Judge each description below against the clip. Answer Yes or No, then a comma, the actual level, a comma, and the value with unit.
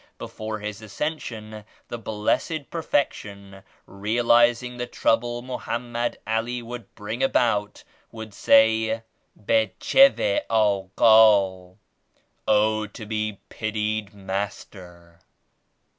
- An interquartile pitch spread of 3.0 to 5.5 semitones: No, narrow, 2.4 semitones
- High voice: No, low, 110 Hz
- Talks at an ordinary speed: No, slow, 85 wpm